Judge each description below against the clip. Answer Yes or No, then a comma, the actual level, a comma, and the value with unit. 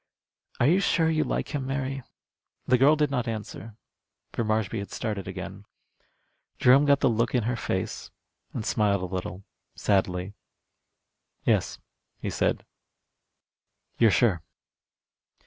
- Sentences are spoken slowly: Yes, slow, 130 wpm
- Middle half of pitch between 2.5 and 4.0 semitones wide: No, average, 5.2 semitones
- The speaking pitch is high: No, low, 115 Hz